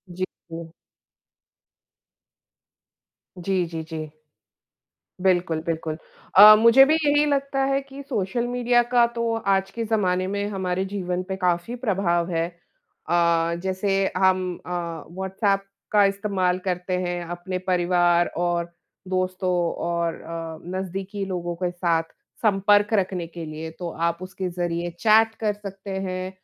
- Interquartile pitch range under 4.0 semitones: Yes, average, 2.8 semitones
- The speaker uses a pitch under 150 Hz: No, medium, 185 Hz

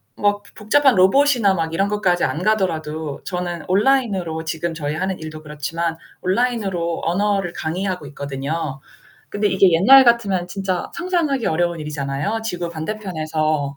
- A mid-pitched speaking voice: Yes, medium, 180 Hz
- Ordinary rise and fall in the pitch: Yes, average, 4.5 semitones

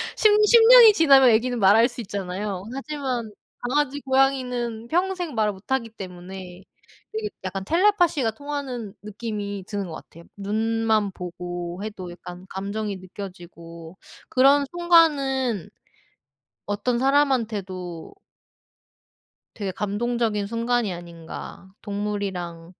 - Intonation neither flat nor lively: No, wide, 5.8 semitones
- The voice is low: No, high, 220 Hz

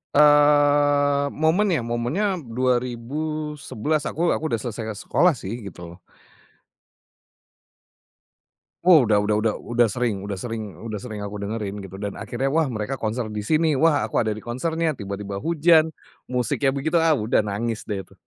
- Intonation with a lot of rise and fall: Yes, wide, 6.0 semitones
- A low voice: Yes, low, 120 Hz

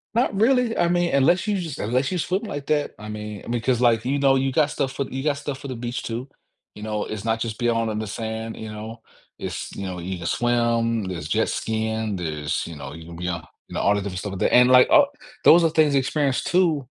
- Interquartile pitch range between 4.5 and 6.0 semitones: Yes, average, 5.1 semitones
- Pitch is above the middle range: No, low, 120 Hz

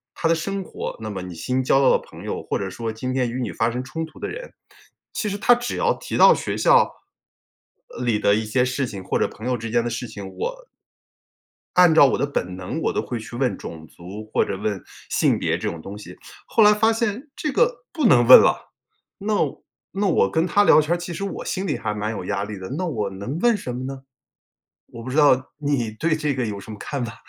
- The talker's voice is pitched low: Yes, low, 130 Hz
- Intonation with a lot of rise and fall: Yes, wide, 8.8 semitones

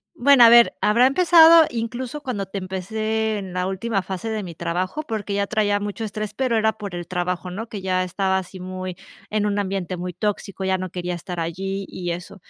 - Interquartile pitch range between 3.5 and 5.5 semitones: No, average, 3.1 semitones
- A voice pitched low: No, high, 200 Hz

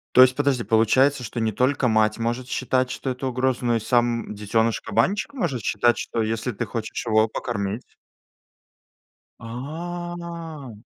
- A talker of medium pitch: No, low, 120 Hz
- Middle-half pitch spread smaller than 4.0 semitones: Yes, average, 3.1 semitones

